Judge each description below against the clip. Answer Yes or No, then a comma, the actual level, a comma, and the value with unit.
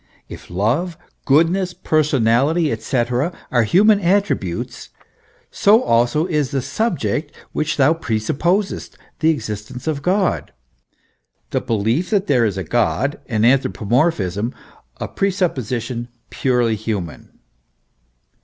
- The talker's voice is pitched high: No, low, 135 Hz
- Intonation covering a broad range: Yes, wide, 6.8 semitones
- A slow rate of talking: Yes, slow, 115 wpm